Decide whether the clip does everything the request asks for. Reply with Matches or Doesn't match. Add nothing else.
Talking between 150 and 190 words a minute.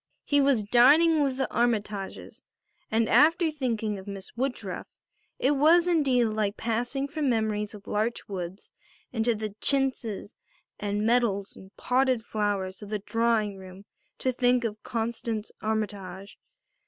Doesn't match